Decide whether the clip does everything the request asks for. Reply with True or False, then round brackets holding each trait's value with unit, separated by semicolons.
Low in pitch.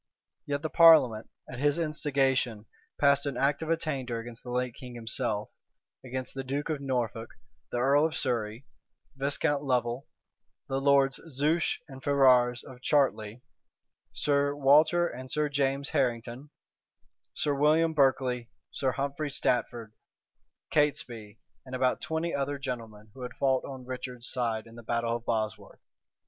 True (130 Hz)